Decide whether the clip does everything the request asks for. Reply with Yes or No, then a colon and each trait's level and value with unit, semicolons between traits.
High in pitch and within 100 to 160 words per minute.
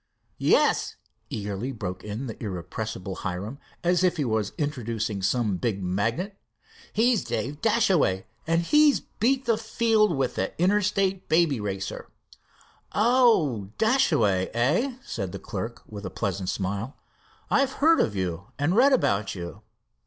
No: low, 125 Hz; average, 140 wpm